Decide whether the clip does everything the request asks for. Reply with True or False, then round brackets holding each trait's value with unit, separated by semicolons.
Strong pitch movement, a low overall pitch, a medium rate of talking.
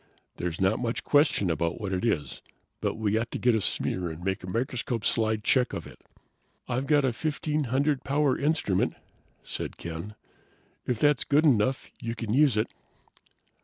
True (5.7 semitones; 115 Hz; 170 wpm)